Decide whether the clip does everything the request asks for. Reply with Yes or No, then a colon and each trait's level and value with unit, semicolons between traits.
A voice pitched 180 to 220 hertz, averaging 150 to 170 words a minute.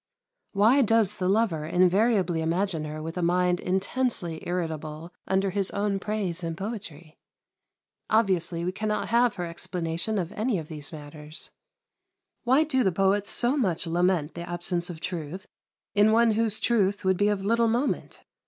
Yes: medium, 185 Hz; average, 160 wpm